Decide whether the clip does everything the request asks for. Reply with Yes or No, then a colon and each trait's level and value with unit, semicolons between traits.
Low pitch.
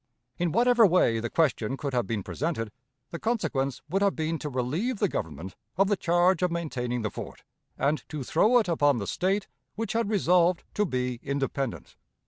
No: medium, 160 Hz